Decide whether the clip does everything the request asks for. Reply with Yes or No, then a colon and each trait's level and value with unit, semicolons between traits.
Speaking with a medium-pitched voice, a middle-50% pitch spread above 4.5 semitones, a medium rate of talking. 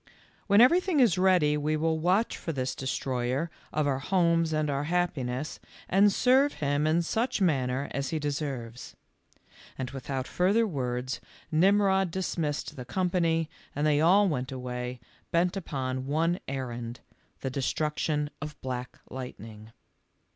Yes: medium, 150 Hz; average, 5.3 semitones; average, 150 wpm